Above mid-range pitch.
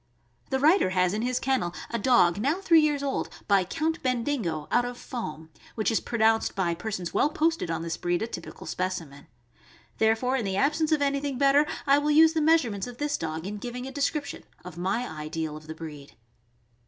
Yes: high, 235 Hz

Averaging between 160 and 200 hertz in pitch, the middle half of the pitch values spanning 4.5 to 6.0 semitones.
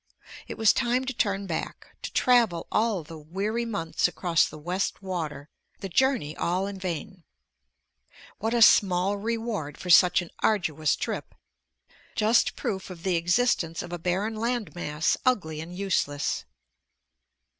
Yes: medium, 185 Hz; average, 4.8 semitones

